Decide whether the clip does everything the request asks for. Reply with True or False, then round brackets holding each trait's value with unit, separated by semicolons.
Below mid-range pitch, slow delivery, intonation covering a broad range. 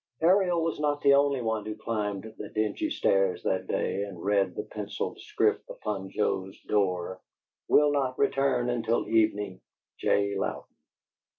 False (110 Hz; 150 wpm; 5.8 semitones)